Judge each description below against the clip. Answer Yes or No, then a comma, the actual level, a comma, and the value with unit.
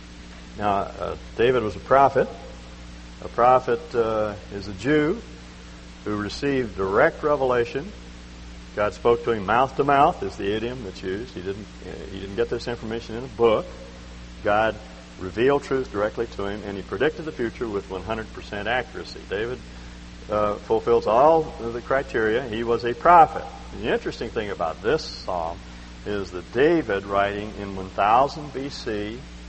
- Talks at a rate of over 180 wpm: No, average, 160 wpm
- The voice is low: Yes, low, 100 Hz